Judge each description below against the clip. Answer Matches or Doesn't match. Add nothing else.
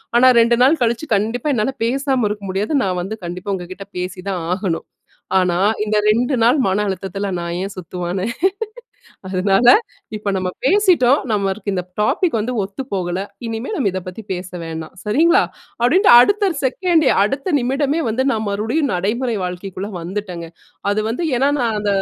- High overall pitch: Matches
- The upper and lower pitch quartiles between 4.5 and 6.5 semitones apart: Matches